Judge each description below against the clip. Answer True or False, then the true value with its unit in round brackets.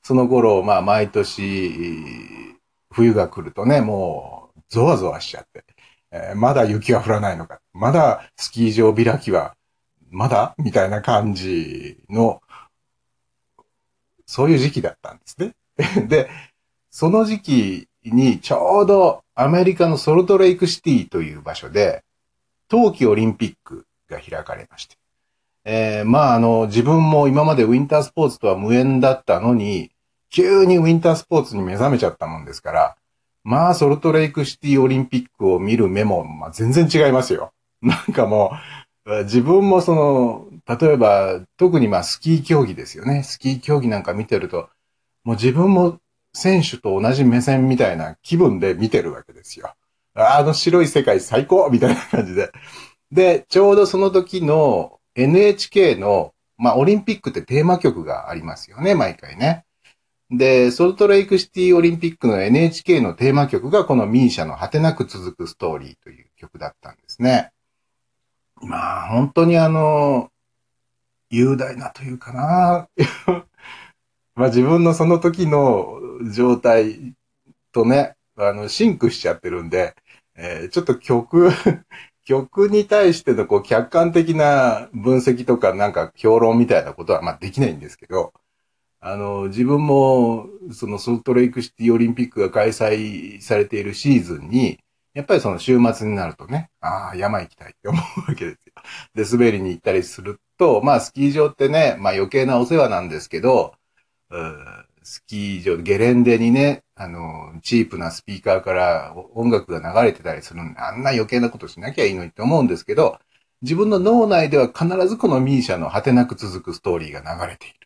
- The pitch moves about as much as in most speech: False (6.4 semitones)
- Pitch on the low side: True (130 Hz)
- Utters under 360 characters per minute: True (330 characters per minute)